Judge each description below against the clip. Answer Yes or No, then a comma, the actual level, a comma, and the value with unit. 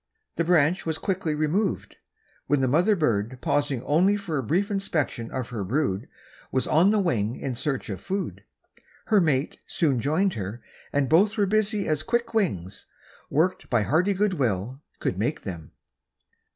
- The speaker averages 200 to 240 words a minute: No, average, 165 wpm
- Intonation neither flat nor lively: No, wide, 7.4 semitones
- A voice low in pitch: No, medium, 155 Hz